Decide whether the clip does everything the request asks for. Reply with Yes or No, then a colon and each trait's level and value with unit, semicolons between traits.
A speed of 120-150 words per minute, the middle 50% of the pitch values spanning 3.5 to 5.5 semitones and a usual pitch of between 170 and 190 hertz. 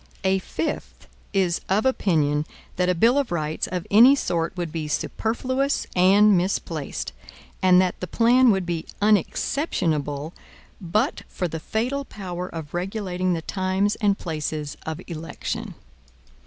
Yes: average, 140 wpm; average, 4.3 semitones; medium, 185 Hz